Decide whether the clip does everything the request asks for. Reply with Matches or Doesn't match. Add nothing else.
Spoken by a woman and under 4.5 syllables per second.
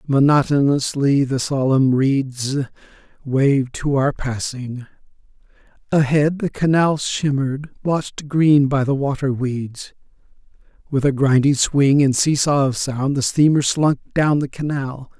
Doesn't match